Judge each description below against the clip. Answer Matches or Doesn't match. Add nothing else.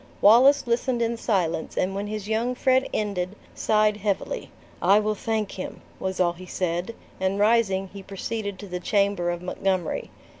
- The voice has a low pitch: Doesn't match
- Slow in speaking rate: Doesn't match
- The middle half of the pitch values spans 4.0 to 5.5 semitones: Doesn't match